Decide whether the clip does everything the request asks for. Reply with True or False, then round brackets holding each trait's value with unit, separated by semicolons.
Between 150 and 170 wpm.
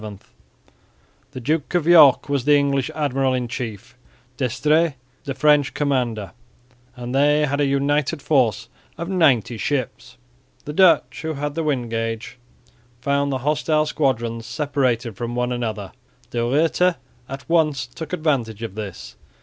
False (140 wpm)